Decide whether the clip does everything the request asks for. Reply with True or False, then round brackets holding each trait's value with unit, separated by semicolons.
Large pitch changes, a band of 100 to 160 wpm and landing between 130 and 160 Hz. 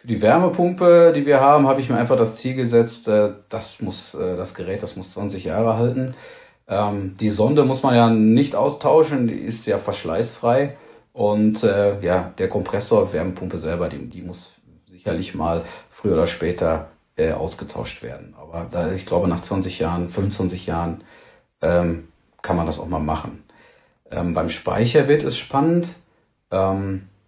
False (6.1 semitones; 150 wpm; 105 Hz)